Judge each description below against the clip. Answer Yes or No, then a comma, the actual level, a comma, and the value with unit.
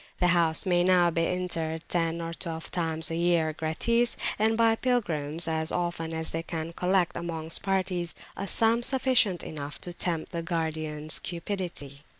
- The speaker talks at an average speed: Yes, average, 155 wpm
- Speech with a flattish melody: Yes, narrow, 2.2 semitones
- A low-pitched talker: No, medium, 170 Hz